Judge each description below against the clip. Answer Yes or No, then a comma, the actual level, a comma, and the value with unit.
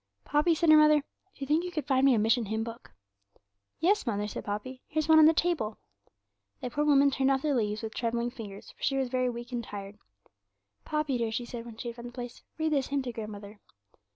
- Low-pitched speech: No, very high, 250 Hz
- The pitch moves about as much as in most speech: Yes, average, 4.6 semitones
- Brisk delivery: Yes, fast, 235 wpm